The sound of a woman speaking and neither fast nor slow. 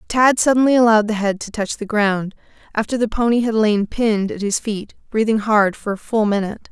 No: female; fast, 215 wpm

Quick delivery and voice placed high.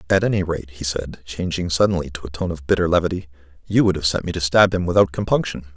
No: fast, 240 wpm; very low, 85 Hz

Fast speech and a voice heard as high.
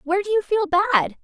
Yes: fast, 245 wpm; very high, 370 Hz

